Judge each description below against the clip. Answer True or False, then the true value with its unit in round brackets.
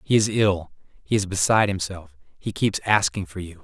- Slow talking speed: False (200 wpm)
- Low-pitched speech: True (95 Hz)